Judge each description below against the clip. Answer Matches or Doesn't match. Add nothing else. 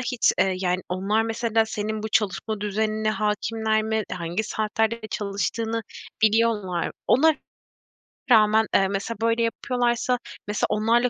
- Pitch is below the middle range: Doesn't match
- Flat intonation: Matches